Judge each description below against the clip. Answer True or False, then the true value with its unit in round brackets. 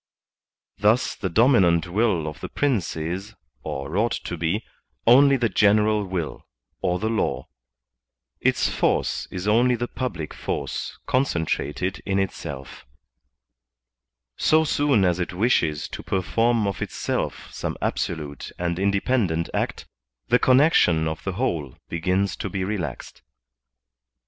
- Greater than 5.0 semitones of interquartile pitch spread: True (5.5 semitones)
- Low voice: True (95 Hz)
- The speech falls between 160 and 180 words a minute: False (135 wpm)